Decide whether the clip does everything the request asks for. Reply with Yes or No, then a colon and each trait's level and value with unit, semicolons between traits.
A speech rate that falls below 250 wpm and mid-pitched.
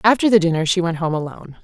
No: fast, 255 wpm; medium, 180 Hz